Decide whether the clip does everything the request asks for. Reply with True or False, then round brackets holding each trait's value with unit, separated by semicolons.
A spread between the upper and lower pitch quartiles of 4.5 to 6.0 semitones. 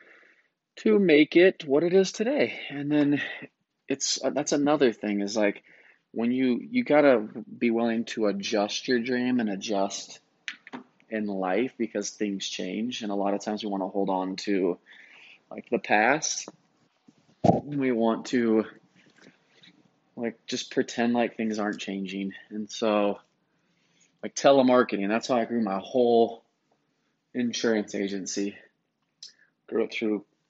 False (3.7 semitones)